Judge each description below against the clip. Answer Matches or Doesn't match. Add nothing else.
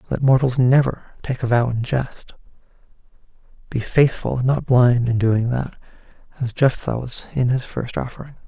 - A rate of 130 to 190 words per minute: Matches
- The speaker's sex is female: Doesn't match